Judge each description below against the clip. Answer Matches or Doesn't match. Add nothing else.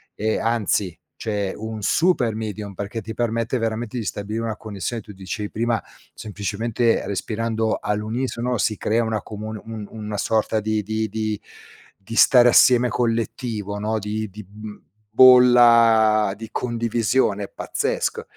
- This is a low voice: Matches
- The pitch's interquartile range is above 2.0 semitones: Doesn't match